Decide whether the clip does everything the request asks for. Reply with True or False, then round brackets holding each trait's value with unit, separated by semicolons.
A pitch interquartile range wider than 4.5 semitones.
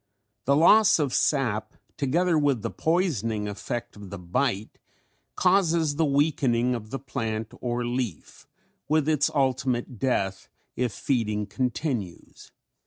True (5.1 semitones)